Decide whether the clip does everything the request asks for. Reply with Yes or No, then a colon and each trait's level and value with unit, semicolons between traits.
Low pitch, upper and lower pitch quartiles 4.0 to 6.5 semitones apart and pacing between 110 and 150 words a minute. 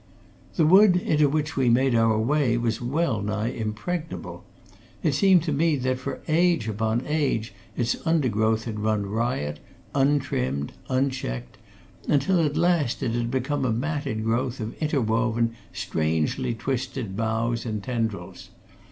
Yes: low, 120 Hz; average, 4.9 semitones; average, 140 wpm